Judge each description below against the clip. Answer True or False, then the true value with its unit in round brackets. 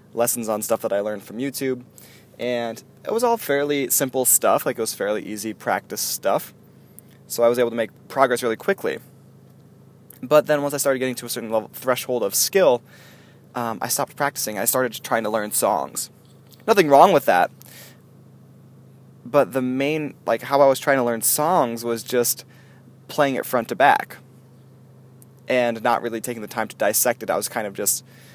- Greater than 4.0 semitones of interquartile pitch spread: False (2.8 semitones)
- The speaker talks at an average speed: True (190 wpm)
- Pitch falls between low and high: False (125 Hz)